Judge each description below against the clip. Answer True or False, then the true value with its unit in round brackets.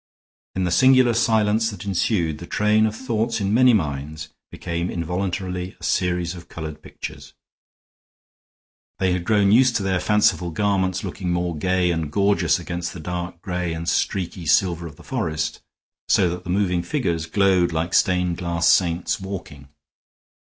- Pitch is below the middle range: True (90 Hz)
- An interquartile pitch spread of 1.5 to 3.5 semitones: True (2.9 semitones)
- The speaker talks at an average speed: True (160 wpm)